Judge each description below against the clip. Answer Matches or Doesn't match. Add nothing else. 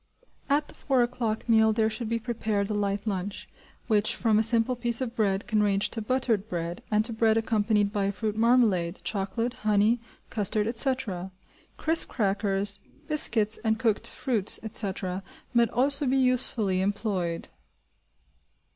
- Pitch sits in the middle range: Doesn't match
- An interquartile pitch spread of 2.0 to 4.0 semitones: Matches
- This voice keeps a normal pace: Matches